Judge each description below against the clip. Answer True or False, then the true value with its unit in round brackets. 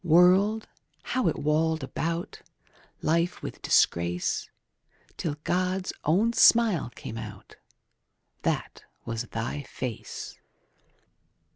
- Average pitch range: False (7.0 semitones)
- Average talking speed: False (100 wpm)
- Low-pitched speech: False (160 Hz)